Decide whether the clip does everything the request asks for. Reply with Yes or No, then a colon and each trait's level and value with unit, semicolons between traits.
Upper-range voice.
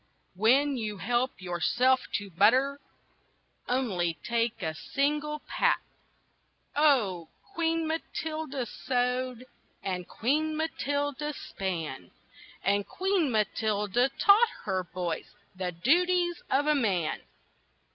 Yes: very high, 250 Hz